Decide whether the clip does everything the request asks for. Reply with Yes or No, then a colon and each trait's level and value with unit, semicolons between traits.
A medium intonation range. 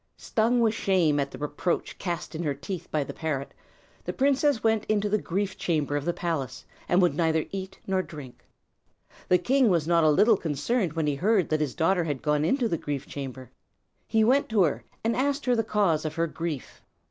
No: wide, 6.2 semitones